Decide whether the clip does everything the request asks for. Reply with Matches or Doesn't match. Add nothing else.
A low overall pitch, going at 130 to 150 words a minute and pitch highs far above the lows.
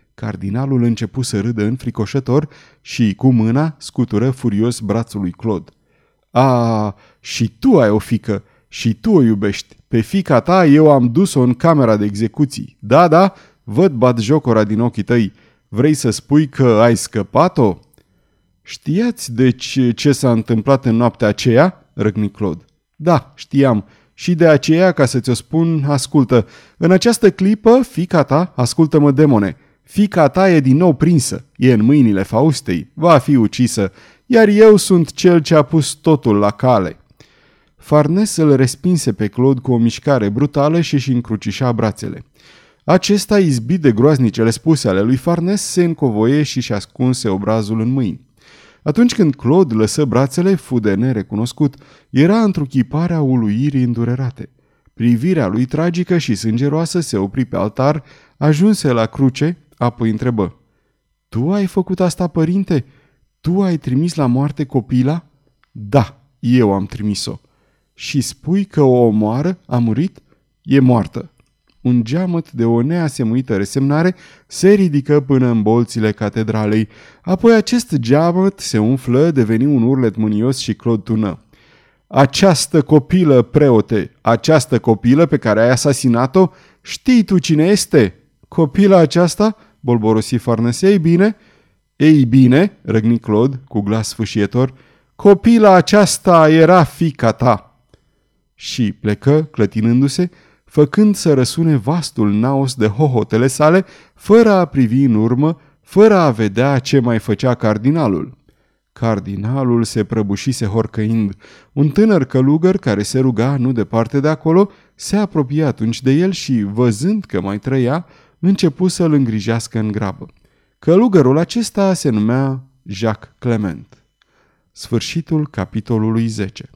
Matches